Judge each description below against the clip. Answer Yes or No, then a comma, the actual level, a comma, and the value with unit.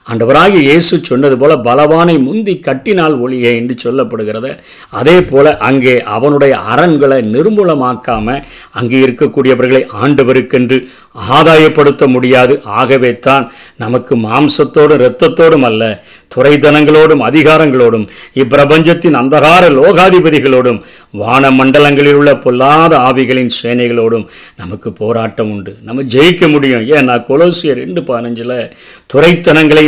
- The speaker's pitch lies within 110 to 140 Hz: Yes, low, 135 Hz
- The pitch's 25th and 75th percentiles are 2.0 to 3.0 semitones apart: No, average, 3.6 semitones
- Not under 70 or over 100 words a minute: Yes, average, 95 wpm